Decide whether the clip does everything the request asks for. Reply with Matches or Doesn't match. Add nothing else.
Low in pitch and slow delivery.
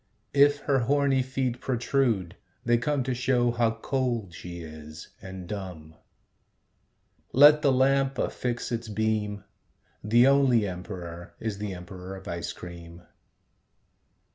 Matches